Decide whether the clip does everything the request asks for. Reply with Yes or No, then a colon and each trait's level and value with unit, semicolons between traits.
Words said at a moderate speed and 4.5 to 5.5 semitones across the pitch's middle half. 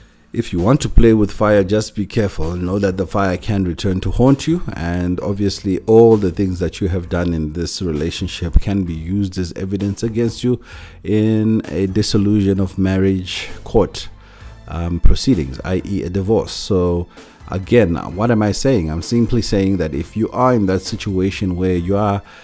No: average, 180 wpm; average, 3.4 semitones